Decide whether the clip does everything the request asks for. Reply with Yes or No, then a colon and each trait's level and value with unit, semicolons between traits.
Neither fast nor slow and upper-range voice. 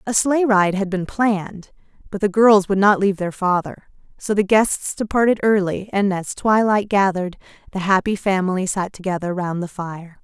Yes: average, 180 wpm; high, 195 Hz